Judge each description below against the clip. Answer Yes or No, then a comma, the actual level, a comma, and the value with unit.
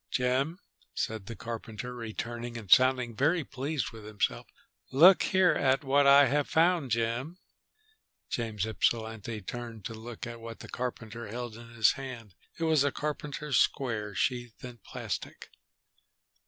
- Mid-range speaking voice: No, low, 120 Hz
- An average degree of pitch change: Yes, average, 3.5 semitones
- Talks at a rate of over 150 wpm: No, average, 145 wpm